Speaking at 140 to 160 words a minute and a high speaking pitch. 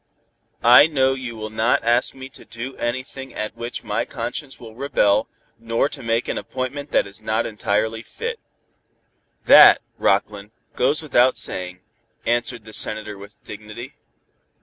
No: average, 150 wpm; low, 115 Hz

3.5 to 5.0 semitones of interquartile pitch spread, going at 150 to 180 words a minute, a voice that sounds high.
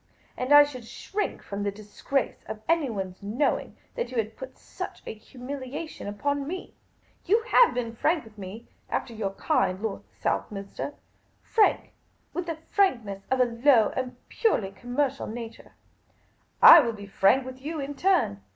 No: wide, 5.4 semitones; average, 160 wpm; very high, 250 Hz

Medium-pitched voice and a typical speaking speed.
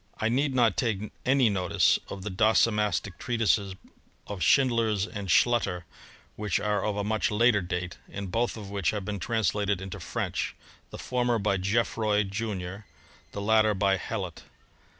No: low, 105 Hz; average, 160 wpm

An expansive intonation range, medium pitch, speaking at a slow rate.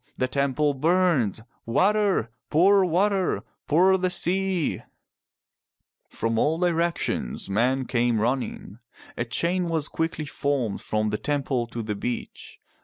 Yes: wide, 7.1 semitones; medium, 145 Hz; slow, 125 wpm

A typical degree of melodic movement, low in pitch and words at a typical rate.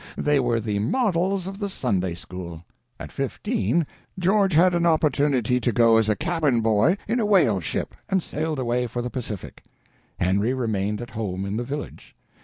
No: wide, 7.9 semitones; low, 125 Hz; average, 170 wpm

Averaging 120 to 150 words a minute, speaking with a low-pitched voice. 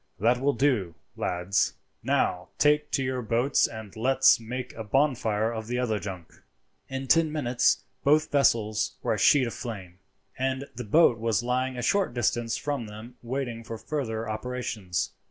No: average, 165 wpm; low, 120 Hz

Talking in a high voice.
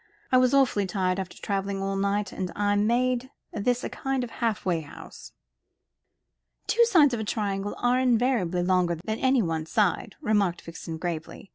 Yes: high, 205 Hz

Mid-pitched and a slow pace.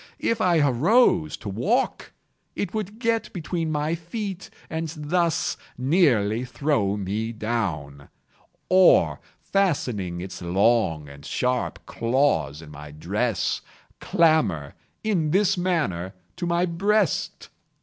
Yes: medium, 145 Hz; slow, 115 wpm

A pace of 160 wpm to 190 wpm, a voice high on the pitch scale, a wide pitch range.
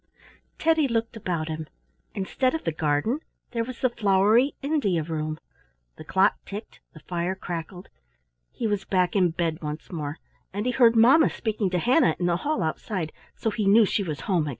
Yes: average, 185 wpm; high, 195 Hz; wide, 5.8 semitones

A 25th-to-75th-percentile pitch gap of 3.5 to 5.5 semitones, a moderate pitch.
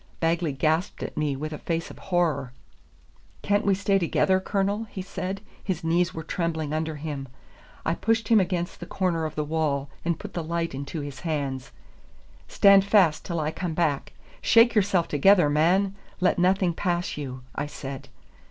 Yes: average, 3.9 semitones; medium, 170 Hz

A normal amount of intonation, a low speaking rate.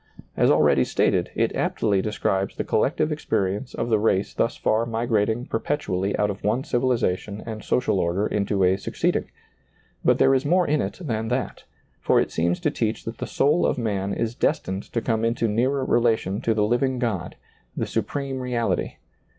No: average, 3.9 semitones; average, 180 wpm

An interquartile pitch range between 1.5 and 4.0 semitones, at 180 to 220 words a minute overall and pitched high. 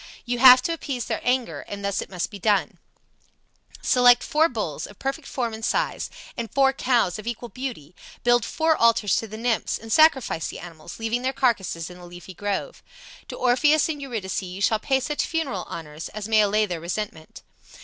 No: average, 4.9 semitones; average, 195 wpm; high, 225 Hz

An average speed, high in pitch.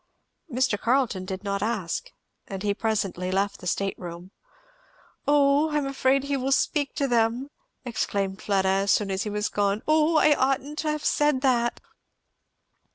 Yes: average, 165 wpm; high, 230 Hz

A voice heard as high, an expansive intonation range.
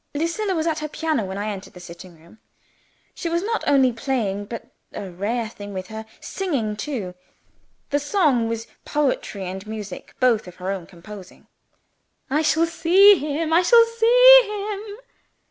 Yes: very high, 255 Hz; wide, 8.8 semitones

